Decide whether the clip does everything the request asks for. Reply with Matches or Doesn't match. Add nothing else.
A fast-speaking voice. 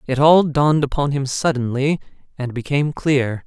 Doesn't match